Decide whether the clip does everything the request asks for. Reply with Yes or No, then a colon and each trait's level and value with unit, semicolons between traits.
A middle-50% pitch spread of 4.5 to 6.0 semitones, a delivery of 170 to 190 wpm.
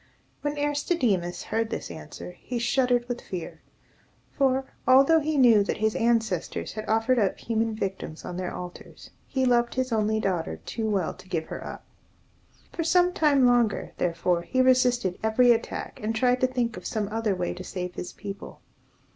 Yes: average, 4.8 semitones; average, 175 wpm